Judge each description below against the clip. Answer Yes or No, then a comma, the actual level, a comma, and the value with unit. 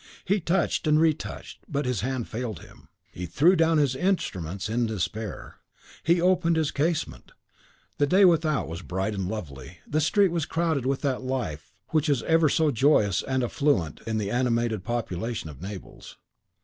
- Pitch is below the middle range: Yes, low, 130 Hz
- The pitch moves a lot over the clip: Yes, wide, 7.2 semitones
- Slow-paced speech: No, average, 170 wpm